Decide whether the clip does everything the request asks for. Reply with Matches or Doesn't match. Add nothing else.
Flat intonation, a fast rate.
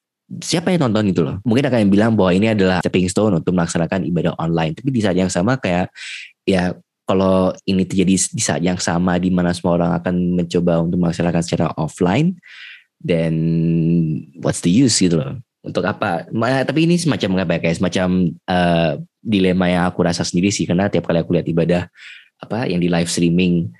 Matches